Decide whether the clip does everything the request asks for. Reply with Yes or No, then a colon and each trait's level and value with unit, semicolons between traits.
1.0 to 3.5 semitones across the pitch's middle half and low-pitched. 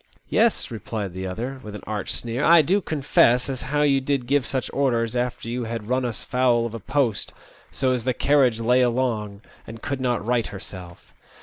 Yes: average, 2.9 semitones; low, 125 Hz